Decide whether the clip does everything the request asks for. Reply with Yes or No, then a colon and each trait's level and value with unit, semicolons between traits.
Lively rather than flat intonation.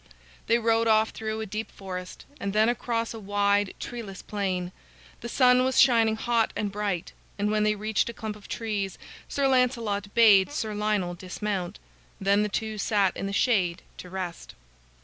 No: narrow, 2.4 semitones